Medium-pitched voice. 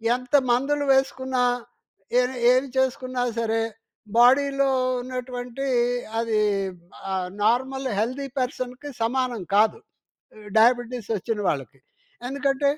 No: very high, 255 Hz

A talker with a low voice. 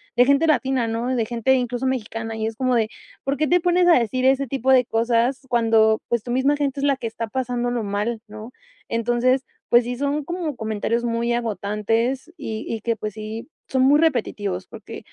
No: high, 240 Hz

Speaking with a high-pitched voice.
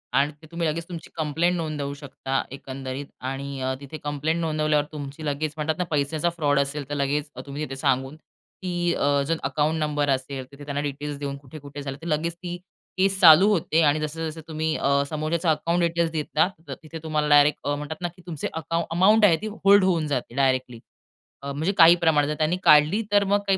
No: medium, 150 Hz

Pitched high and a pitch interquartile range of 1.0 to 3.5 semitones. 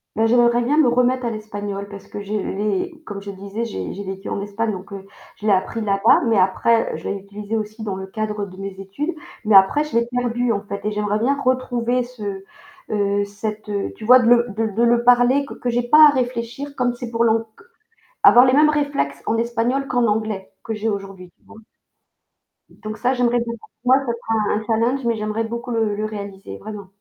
Yes: high, 225 Hz; average, 3.2 semitones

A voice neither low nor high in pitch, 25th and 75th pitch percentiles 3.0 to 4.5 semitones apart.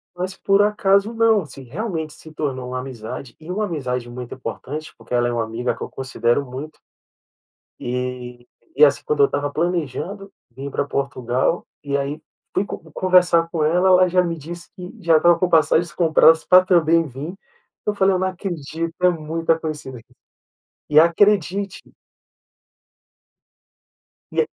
No: medium, 160 Hz; wide, 5.4 semitones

